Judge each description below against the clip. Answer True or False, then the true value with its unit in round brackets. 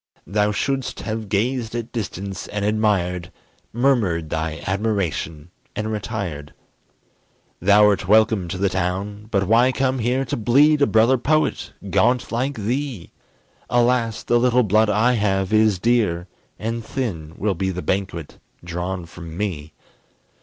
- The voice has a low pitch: True (105 Hz)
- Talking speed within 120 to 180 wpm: True (140 wpm)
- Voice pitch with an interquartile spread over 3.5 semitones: True (4.3 semitones)